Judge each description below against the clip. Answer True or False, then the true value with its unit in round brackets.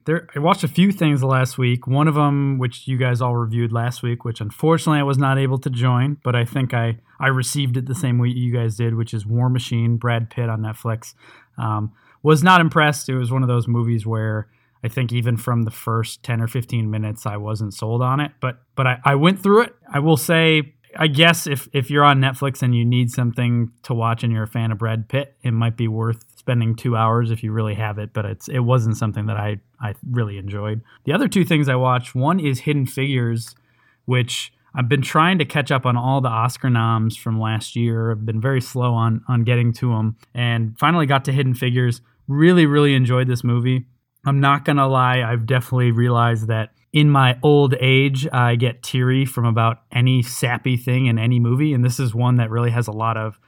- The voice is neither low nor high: False (125 Hz)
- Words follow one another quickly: True (230 wpm)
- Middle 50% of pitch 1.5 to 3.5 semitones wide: True (2.8 semitones)